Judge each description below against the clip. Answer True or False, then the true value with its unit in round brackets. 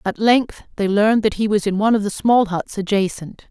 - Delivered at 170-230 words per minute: False (240 wpm)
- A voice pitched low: False (205 Hz)